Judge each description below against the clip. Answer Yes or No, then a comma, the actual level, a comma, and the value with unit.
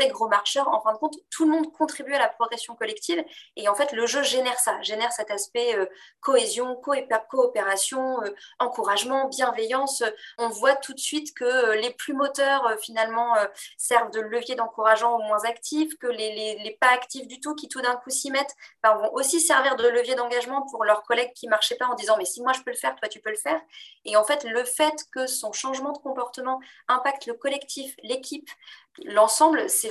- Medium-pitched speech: No, very high, 250 Hz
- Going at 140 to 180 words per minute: No, average, 215 wpm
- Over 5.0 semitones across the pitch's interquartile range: No, average, 3.9 semitones